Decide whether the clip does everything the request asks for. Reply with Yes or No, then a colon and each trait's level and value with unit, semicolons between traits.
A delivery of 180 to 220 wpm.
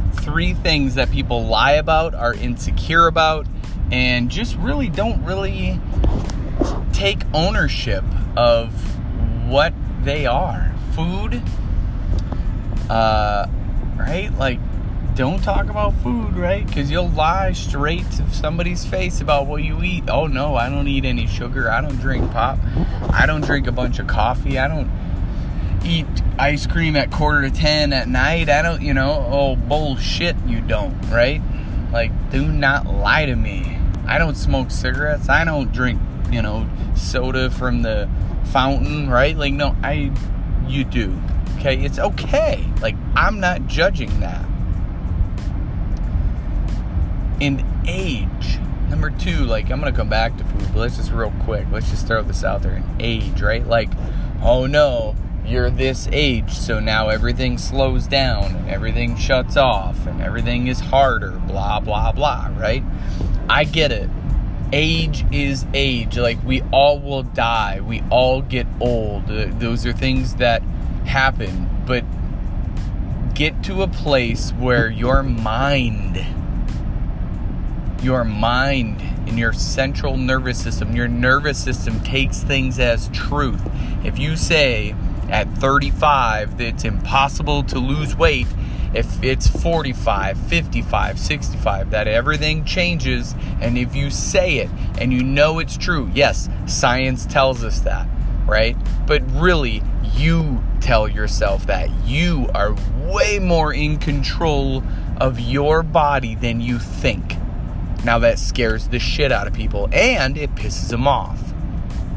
No: average, 145 wpm